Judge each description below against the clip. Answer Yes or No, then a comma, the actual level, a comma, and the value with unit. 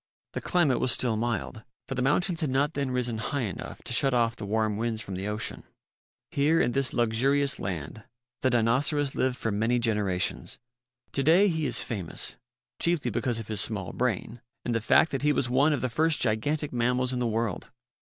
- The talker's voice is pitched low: Yes, low, 125 Hz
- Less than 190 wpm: No, average, 200 wpm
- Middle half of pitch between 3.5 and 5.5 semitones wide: Yes, average, 4.0 semitones